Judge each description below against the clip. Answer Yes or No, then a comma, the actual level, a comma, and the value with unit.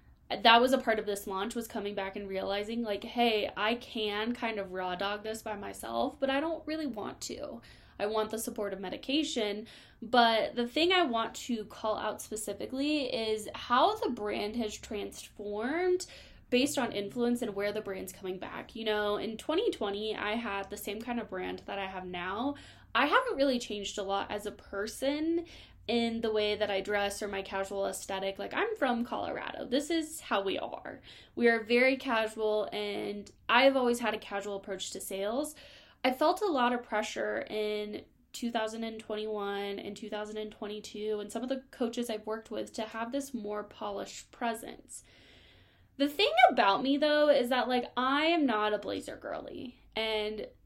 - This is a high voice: Yes, high, 220 Hz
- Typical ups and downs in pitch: Yes, average, 3.5 semitones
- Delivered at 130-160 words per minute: No, average, 180 wpm